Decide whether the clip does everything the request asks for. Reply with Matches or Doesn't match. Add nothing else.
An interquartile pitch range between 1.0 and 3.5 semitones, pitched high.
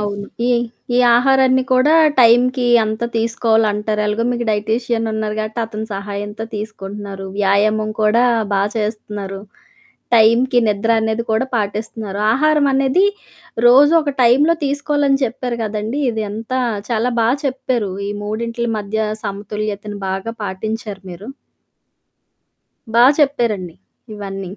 Matches